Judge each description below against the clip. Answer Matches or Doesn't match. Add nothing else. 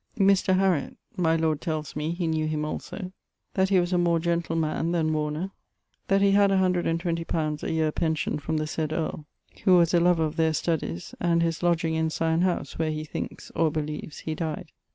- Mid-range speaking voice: Matches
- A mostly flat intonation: Matches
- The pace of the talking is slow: Doesn't match